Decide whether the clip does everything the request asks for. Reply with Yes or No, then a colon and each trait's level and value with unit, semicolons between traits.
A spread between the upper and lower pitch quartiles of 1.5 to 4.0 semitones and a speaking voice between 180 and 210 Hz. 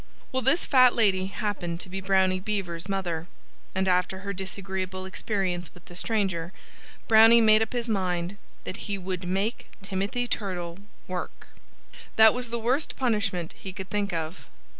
Yes: average, 3.1 semitones; high, 190 Hz